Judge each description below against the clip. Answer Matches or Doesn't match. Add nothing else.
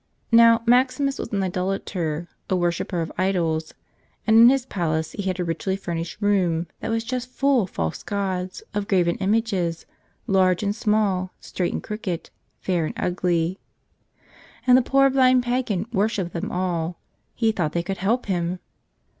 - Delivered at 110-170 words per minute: Matches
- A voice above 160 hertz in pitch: Matches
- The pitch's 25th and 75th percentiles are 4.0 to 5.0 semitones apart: Matches